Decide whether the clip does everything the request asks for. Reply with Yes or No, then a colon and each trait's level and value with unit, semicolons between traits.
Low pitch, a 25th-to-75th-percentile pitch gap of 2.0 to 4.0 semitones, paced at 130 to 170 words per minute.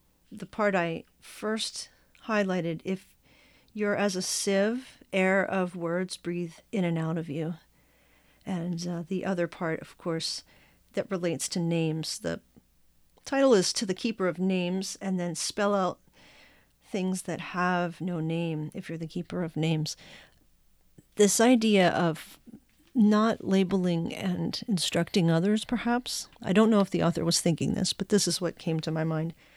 No: medium, 180 Hz; average, 3.1 semitones; average, 160 wpm